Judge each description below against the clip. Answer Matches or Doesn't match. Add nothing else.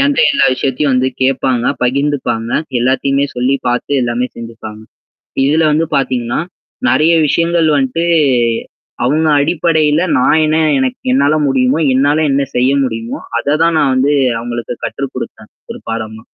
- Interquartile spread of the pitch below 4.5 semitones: Matches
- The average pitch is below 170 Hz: Matches